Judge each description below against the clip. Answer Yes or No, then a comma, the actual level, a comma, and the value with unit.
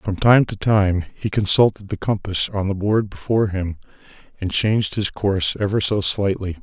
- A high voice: No, low, 100 Hz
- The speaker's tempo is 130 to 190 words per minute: Yes, average, 180 wpm